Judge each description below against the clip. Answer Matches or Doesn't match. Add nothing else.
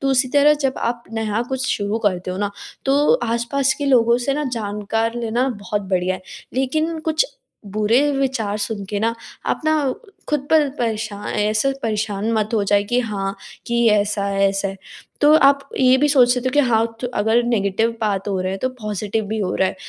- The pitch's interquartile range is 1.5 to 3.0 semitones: Doesn't match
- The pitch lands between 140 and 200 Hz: Doesn't match